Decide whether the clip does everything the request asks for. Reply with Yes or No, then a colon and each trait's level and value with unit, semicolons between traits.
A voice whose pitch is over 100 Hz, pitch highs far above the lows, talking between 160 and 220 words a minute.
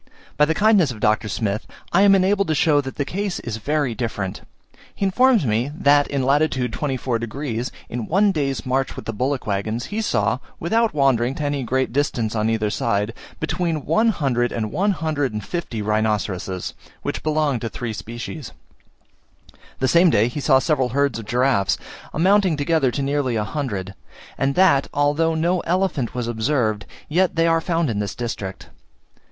Yes: low, 135 Hz; wide, 5.9 semitones; average, 180 wpm